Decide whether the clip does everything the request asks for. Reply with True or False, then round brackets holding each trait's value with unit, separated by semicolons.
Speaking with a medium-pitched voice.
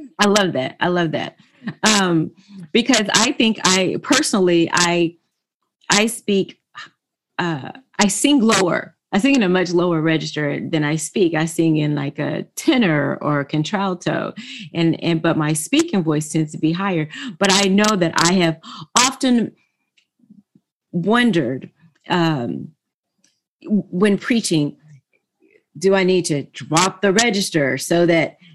True (180 Hz)